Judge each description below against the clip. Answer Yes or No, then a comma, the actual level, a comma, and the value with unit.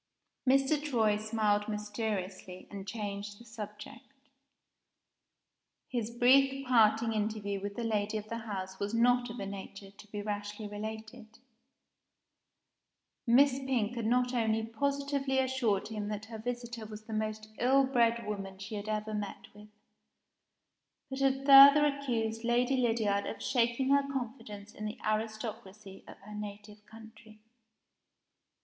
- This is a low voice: No, high, 220 Hz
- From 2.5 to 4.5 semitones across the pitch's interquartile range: Yes, average, 2.9 semitones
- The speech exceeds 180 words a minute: No, average, 140 wpm